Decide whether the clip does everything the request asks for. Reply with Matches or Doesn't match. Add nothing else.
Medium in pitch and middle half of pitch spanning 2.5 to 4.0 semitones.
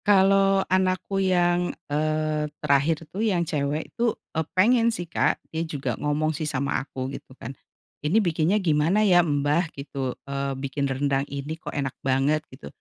Doesn't match